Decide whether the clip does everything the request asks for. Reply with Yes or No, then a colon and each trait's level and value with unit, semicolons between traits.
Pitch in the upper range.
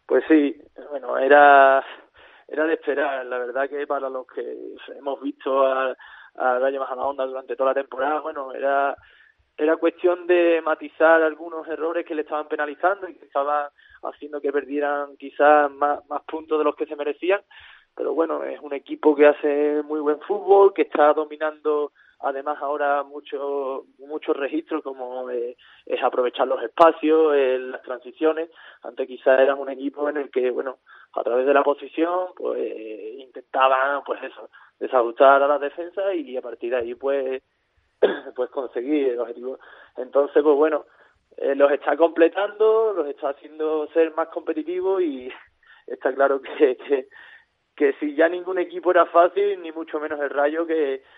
No: medium, 150 Hz